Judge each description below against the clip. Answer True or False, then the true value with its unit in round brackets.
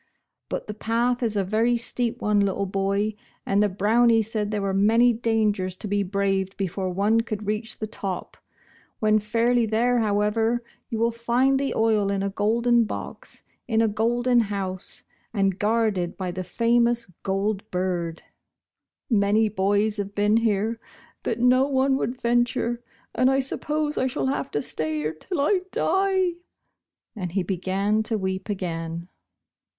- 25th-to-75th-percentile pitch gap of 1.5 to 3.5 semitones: True (3.2 semitones)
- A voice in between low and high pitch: False (215 Hz)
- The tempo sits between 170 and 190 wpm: False (160 wpm)